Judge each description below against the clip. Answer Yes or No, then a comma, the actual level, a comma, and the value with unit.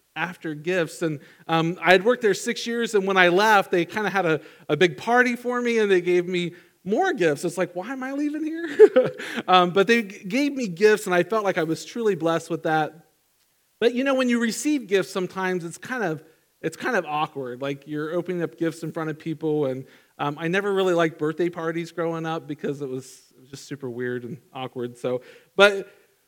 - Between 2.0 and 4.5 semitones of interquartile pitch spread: No, average, 5.3 semitones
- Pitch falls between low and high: Yes, medium, 180 Hz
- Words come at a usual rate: No, fast, 230 wpm